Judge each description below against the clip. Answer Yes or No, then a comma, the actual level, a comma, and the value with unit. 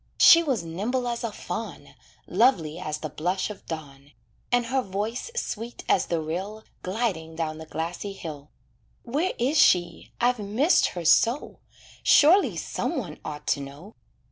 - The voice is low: No, high, 195 Hz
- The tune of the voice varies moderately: No, wide, 6.9 semitones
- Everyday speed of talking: Yes, average, 155 wpm